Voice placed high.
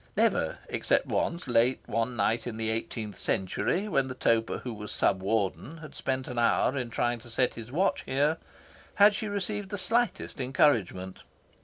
No: low, 125 Hz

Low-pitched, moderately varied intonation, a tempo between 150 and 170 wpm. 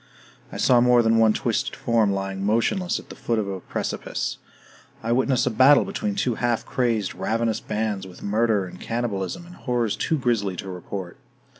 No: low, 115 Hz; average, 3.6 semitones; average, 180 wpm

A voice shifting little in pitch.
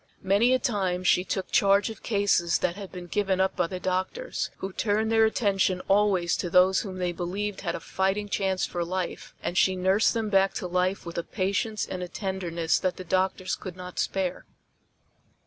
Yes: narrow, 1.9 semitones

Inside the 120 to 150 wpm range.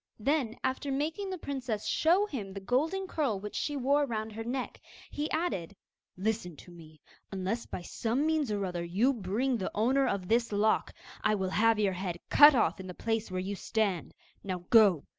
No: average, 200 wpm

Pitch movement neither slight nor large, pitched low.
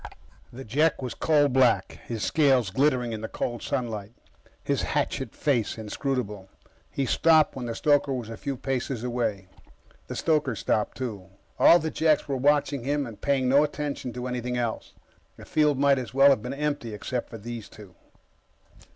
Yes: average, 3.5 semitones; low, 130 Hz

